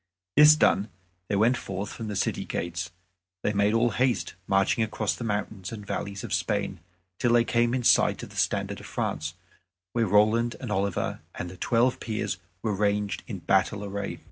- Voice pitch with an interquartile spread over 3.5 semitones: No, average, 3.0 semitones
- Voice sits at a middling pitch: No, low, 105 Hz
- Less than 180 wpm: No, average, 185 wpm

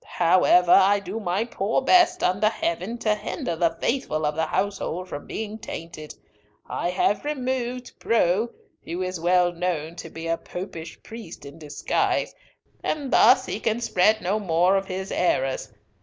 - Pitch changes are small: No, average, 4.7 semitones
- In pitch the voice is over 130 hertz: Yes, medium, 185 Hz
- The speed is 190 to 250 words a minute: No, average, 160 wpm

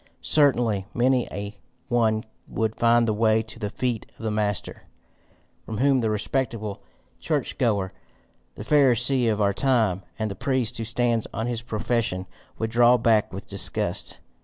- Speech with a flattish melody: Yes, narrow, 2.3 semitones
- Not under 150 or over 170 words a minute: Yes, average, 160 wpm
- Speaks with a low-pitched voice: Yes, low, 115 Hz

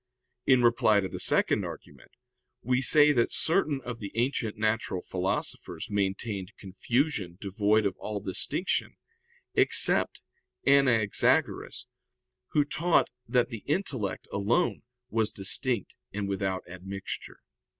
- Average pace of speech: No, slow, 115 wpm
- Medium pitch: No, low, 110 Hz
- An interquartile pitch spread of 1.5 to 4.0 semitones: No, average, 4.6 semitones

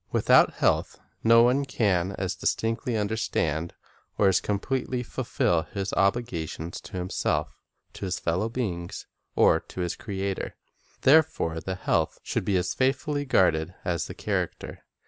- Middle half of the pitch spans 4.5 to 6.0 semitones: Yes, average, 4.8 semitones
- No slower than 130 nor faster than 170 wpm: Yes, average, 145 wpm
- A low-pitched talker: Yes, very low, 95 Hz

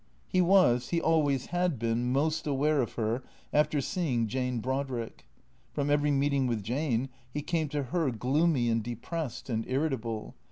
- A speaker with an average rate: Yes, average, 160 wpm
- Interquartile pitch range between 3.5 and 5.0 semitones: Yes, average, 4.2 semitones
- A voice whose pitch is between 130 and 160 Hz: Yes, low, 135 Hz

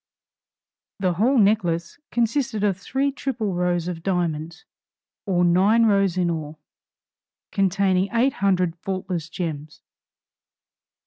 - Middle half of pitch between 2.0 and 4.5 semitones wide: Yes, average, 3.4 semitones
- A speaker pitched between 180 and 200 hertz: Yes, medium, 185 Hz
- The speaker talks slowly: Yes, slow, 110 wpm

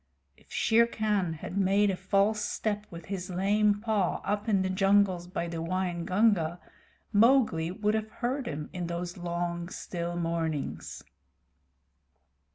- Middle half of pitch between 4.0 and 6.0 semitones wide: No, average, 3.3 semitones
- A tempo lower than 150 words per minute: Yes, average, 140 wpm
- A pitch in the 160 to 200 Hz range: Yes, high, 190 Hz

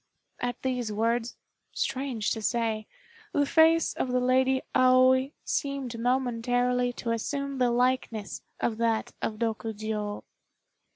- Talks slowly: Yes, slow, 120 wpm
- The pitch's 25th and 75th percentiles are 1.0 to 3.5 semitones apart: Yes, narrow, 2.4 semitones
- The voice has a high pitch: Yes, high, 245 Hz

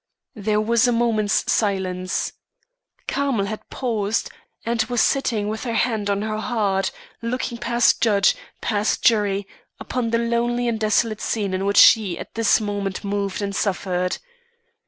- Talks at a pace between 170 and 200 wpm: No, average, 150 wpm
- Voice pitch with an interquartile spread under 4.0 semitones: Yes, narrow, 2.6 semitones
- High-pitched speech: Yes, high, 215 Hz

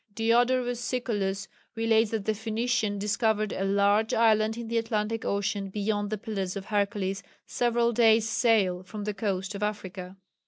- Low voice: No, high, 215 Hz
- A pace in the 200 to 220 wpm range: No, average, 155 wpm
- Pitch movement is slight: Yes, narrow, 2.2 semitones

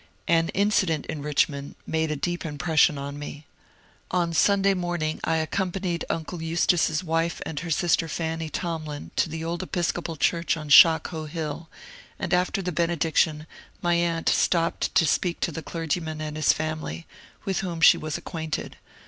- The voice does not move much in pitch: Yes, narrow, 1.9 semitones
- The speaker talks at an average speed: Yes, average, 160 wpm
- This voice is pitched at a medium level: Yes, medium, 165 Hz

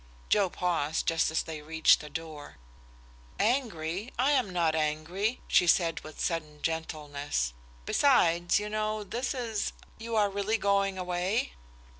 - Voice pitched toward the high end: No, medium, 180 Hz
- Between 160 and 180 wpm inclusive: No, average, 140 wpm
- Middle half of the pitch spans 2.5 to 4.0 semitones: No, average, 5.0 semitones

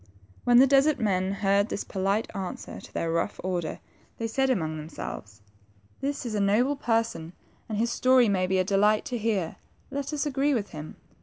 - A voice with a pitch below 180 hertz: No, high, 210 Hz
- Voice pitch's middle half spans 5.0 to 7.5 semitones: Yes, average, 5.3 semitones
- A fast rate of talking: No, average, 190 wpm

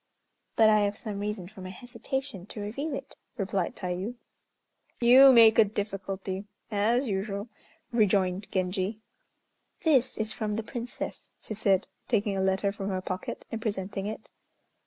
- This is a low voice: No, high, 205 Hz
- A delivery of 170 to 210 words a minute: No, average, 150 wpm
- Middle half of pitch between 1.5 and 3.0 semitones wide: Yes, average, 2.7 semitones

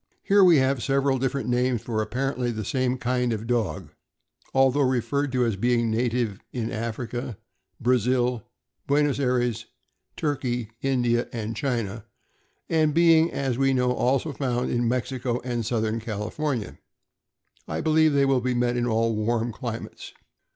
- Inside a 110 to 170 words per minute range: Yes, average, 150 wpm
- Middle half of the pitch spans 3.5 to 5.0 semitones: No, narrow, 2.6 semitones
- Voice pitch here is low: Yes, low, 125 Hz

